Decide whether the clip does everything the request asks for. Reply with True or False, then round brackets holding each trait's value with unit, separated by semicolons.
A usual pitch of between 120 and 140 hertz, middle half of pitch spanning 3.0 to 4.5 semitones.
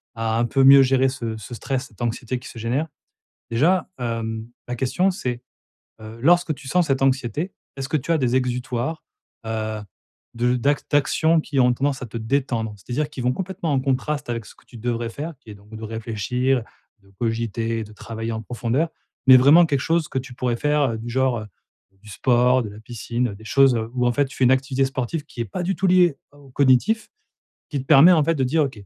True (130 Hz; 3.6 semitones)